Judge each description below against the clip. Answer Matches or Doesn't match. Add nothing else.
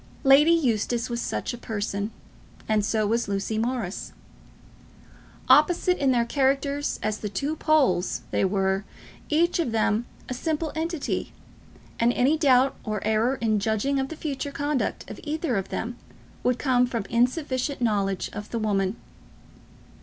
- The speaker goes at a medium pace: Matches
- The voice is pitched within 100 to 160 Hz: Doesn't match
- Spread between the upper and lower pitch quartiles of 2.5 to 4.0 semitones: Doesn't match